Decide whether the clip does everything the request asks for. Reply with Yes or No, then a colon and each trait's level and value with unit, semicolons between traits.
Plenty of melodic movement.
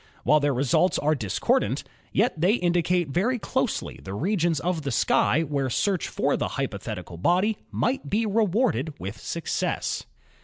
Yes: wide, 6.5 semitones